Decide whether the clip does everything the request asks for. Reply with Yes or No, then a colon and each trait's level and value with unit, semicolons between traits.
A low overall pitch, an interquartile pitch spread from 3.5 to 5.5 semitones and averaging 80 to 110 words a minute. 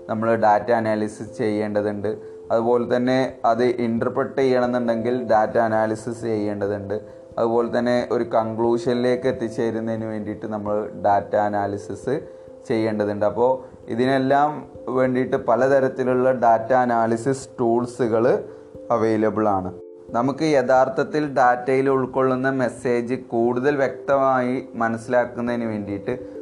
No: low, 120 Hz; average, 3.0 semitones; average, 90 wpm